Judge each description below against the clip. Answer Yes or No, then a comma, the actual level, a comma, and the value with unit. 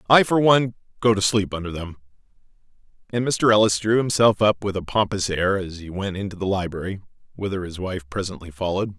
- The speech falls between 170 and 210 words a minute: Yes, average, 195 wpm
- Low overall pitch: Yes, low, 100 Hz